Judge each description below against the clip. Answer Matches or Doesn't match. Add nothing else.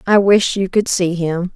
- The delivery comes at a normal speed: Doesn't match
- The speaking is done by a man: Doesn't match